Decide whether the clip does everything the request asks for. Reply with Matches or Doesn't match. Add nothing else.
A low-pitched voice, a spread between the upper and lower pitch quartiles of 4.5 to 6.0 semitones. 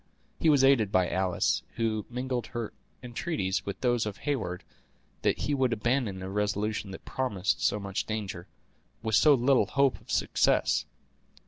Matches